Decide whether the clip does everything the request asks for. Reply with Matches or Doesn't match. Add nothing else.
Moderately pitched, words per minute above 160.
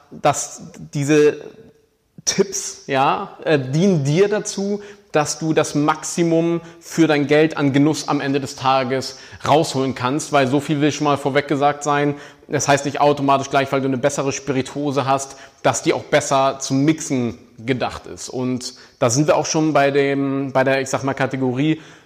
Matches